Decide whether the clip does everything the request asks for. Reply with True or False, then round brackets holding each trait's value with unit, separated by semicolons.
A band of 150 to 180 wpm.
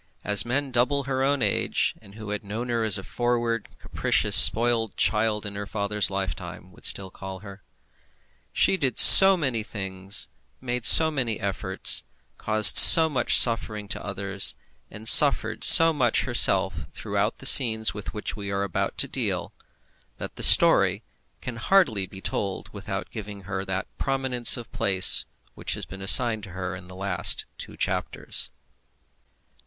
True (160 wpm)